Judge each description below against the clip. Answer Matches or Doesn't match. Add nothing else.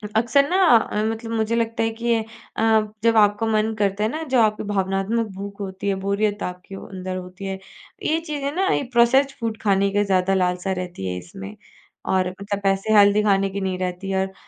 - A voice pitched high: Matches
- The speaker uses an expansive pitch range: Doesn't match